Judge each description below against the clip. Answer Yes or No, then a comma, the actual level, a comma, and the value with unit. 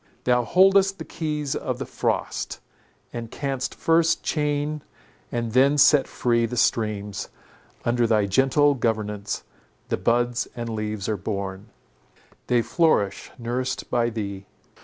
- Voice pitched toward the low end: Yes, low, 120 Hz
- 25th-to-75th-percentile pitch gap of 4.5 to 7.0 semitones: Yes, average, 5.1 semitones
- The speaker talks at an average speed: No, slow, 130 wpm